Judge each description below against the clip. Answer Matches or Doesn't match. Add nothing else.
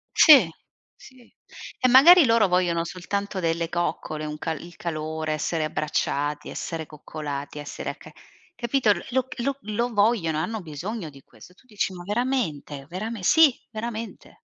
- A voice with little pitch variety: Doesn't match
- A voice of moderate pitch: Matches